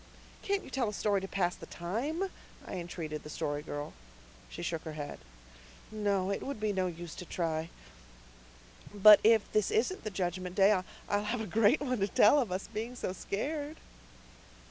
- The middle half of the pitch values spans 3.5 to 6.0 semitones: Yes, average, 4.4 semitones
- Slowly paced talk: No, average, 190 wpm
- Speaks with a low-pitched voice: No, high, 200 Hz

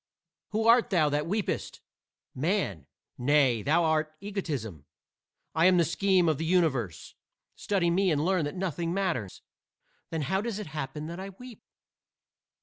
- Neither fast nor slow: Yes, average, 150 wpm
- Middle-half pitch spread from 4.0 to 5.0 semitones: Yes, average, 4.5 semitones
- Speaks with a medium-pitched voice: Yes, medium, 170 Hz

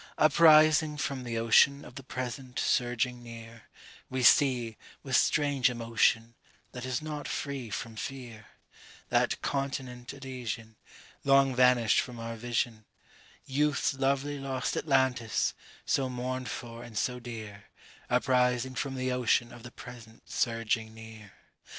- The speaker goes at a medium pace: No, slow, 130 wpm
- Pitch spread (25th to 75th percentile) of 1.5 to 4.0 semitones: Yes, narrow, 2.6 semitones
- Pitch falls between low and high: No, low, 125 Hz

